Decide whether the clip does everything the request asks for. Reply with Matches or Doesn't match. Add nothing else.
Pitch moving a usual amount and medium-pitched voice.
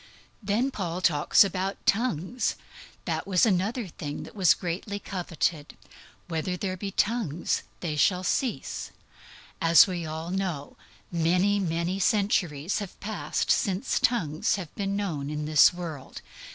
Matches